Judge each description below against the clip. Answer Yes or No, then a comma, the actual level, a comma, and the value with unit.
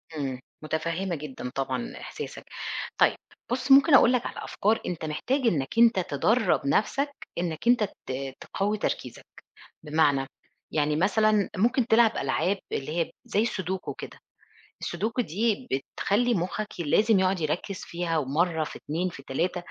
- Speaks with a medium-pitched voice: Yes, medium, 180 Hz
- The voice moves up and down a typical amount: No, wide, 6.2 semitones